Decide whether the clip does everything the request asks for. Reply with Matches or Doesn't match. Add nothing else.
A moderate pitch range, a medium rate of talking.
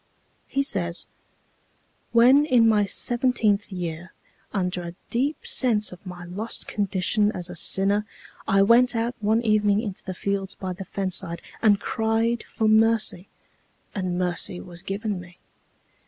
Matches